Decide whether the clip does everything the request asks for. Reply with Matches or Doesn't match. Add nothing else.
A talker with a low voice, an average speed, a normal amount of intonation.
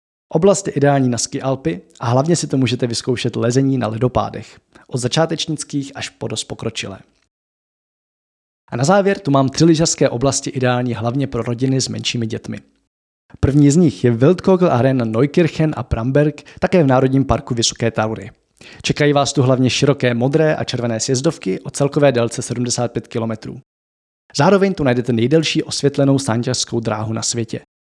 Matches